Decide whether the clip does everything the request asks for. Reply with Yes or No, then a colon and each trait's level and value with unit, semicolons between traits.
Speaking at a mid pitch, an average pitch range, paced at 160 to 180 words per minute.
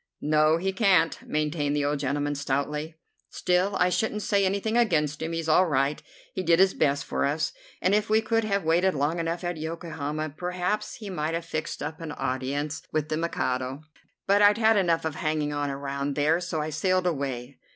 No: medium, 160 Hz; average, 3.9 semitones; average, 200 wpm